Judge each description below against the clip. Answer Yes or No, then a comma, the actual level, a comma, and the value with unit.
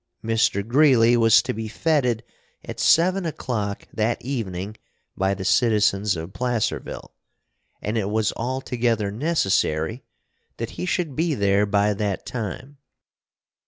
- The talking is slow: Yes, slow, 125 wpm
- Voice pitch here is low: Yes, low, 115 Hz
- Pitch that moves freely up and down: No, average, 4.0 semitones